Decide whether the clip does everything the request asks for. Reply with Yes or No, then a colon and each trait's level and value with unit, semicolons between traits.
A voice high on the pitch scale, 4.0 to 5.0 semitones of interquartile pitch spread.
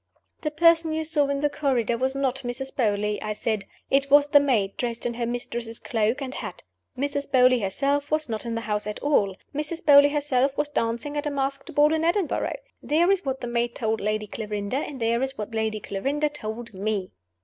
Yes: very high, 260 Hz; average, 4.5 semitones